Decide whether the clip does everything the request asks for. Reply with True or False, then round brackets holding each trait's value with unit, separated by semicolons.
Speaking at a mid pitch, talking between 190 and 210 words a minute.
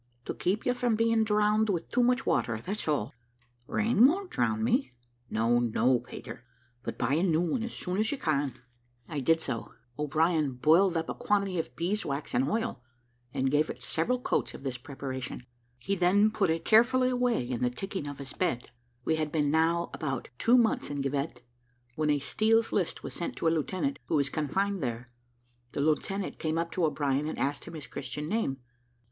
True (160 Hz; 200 wpm)